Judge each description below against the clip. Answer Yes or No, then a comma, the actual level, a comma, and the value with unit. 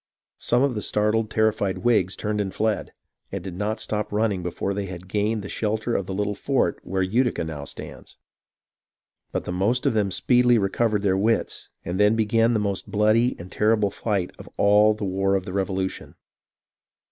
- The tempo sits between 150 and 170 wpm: No, average, 190 wpm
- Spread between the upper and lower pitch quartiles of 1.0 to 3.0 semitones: Yes, narrow, 2.4 semitones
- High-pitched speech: No, low, 105 Hz